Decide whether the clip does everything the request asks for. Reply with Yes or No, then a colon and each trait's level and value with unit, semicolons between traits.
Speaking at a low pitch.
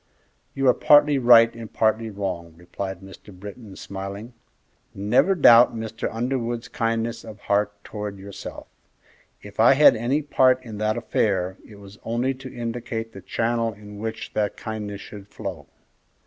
Yes: low, 110 Hz